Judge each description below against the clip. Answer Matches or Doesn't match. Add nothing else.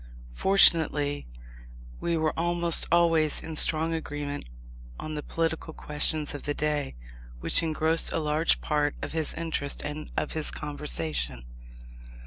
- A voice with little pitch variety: Matches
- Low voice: Doesn't match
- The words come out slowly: Matches